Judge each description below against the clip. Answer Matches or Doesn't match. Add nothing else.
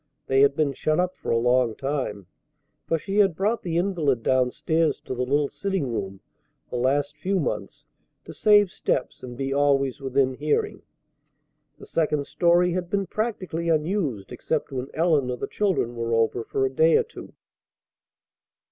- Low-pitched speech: Doesn't match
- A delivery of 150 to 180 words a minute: Matches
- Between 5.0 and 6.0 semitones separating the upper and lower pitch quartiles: Matches